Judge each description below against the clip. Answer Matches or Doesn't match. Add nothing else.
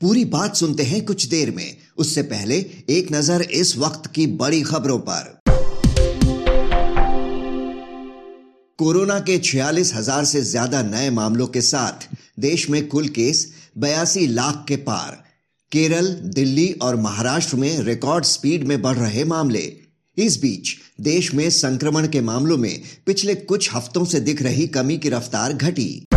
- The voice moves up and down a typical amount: Matches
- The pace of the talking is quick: Doesn't match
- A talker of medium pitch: Matches